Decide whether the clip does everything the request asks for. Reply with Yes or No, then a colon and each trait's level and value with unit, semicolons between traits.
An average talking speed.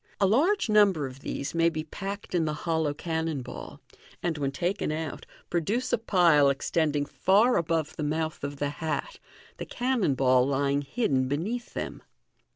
Yes: average, 170 wpm